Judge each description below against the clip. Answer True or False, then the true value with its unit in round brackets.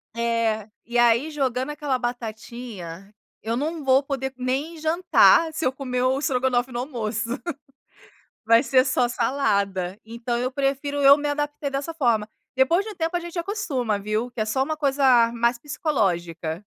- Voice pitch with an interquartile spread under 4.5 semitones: True (3.9 semitones)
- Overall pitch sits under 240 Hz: False (255 Hz)